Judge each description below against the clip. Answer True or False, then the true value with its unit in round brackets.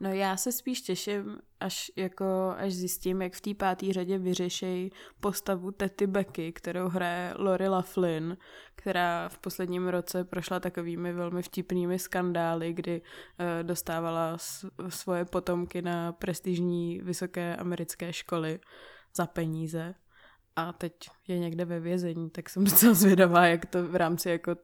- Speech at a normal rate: True (140 wpm)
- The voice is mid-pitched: True (180 Hz)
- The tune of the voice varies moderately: False (1.4 semitones)